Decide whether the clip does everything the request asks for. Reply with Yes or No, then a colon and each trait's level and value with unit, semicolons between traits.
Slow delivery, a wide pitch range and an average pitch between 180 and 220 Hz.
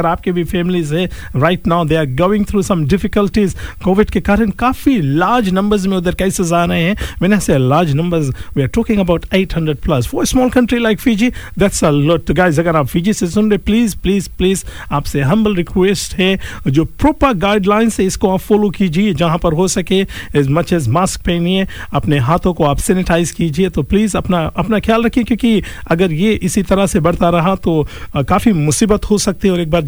No: slow, 100 wpm; average, 3.5 semitones; medium, 185 Hz